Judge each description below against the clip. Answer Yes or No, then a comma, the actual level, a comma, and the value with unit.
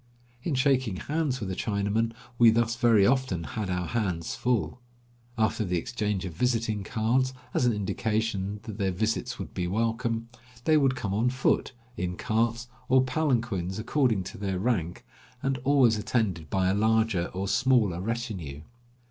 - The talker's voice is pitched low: Yes, low, 110 Hz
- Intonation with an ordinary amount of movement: Yes, average, 4.4 semitones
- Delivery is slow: No, average, 160 wpm